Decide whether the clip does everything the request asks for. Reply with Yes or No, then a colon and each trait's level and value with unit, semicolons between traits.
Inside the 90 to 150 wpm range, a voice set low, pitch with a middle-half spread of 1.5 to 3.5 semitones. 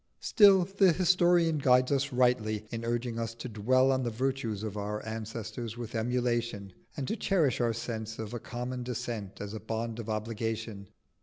No: average, 175 wpm; low, 120 Hz; narrow, 2.6 semitones